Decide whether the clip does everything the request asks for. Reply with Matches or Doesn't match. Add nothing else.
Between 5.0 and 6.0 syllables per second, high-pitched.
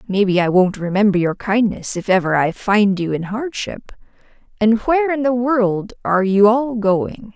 Doesn't match